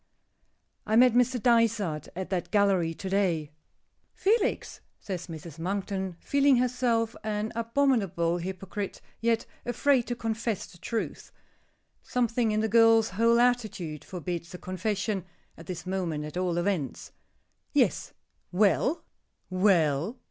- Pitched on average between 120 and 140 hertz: No, high, 205 Hz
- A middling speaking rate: No, slow, 125 wpm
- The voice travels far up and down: No, average, 4.6 semitones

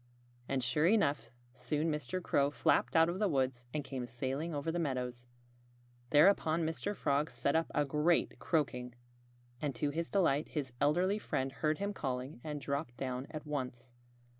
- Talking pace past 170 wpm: No, average, 165 wpm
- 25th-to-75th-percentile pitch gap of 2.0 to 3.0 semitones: No, average, 3.7 semitones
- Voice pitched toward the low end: No, medium, 145 Hz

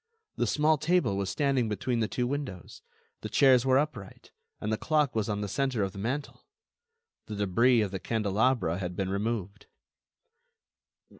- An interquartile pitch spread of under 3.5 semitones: No, average, 5.0 semitones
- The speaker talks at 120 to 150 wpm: No, average, 165 wpm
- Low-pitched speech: Yes, low, 110 Hz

